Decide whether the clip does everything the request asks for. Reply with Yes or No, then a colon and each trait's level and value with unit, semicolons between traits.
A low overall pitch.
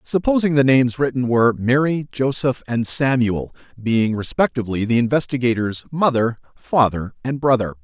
Yes: low, 125 Hz